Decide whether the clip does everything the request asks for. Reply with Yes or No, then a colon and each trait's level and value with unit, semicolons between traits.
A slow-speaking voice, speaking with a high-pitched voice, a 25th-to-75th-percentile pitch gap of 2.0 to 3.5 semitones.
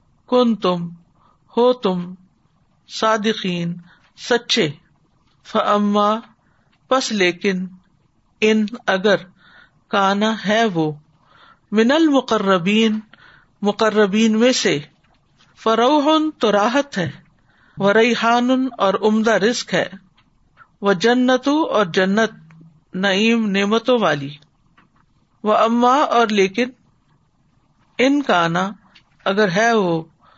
No: slow, 90 wpm; high, 210 Hz; average, 4.2 semitones